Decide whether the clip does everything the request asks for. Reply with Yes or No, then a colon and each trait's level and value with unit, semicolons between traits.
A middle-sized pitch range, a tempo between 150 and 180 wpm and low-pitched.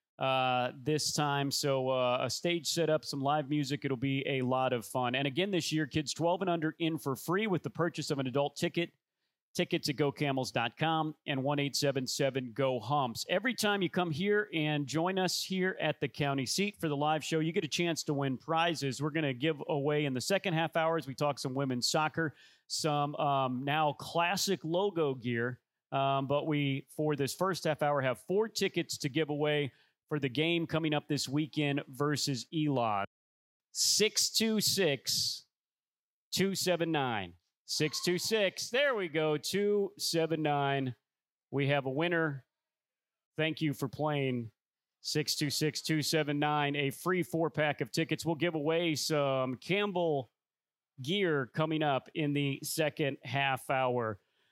No: average, 3.0 semitones; average, 160 wpm; medium, 150 Hz